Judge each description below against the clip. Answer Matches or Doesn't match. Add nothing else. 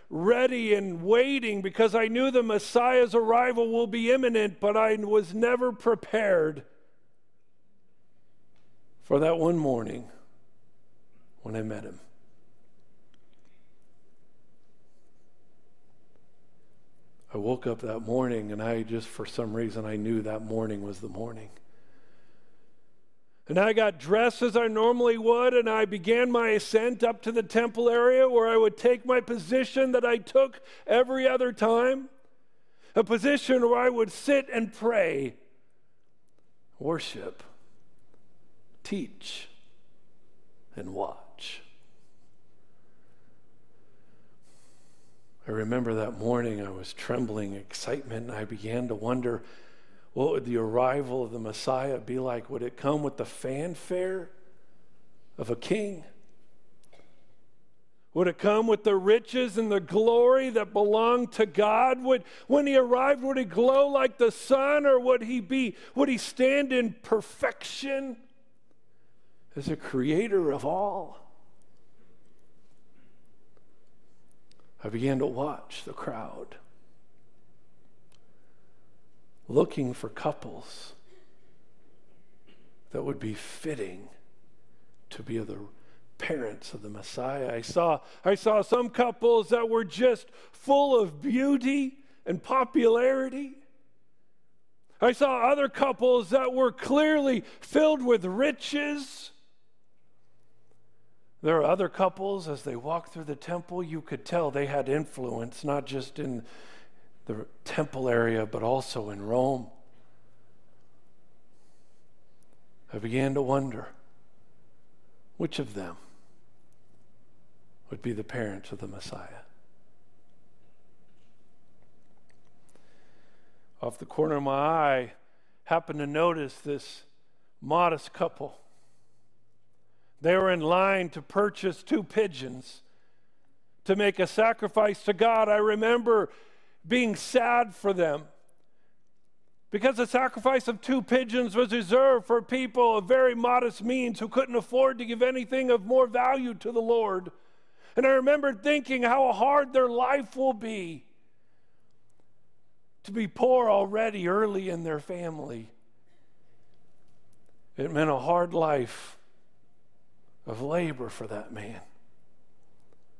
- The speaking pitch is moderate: Doesn't match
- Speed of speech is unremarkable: Doesn't match